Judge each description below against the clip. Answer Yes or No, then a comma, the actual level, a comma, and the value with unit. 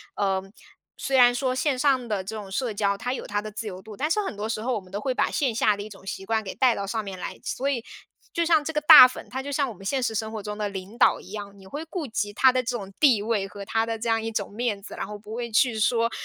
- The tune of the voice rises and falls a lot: No, average, 3.8 semitones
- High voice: Yes, high, 225 Hz